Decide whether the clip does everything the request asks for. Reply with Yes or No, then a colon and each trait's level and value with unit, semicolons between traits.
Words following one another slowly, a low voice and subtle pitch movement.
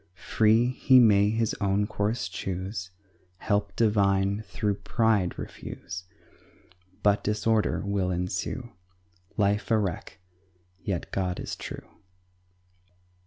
Yes: slow, 105 wpm; low, 100 Hz; narrow, 2.2 semitones